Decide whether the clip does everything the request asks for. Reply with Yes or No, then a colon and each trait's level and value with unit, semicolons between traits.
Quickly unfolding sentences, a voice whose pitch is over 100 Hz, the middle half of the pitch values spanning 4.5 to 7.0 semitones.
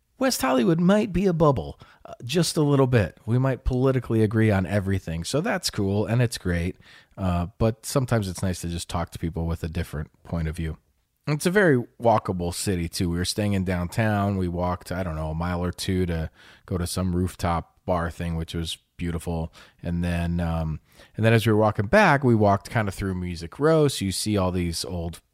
No: fast, 220 wpm; very low, 95 Hz; average, 5.1 semitones